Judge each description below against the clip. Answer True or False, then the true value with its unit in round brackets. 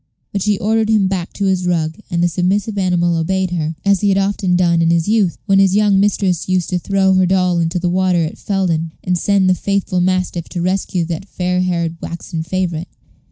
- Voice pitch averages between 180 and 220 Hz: True (185 Hz)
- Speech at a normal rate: False (215 wpm)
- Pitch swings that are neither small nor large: False (2.2 semitones)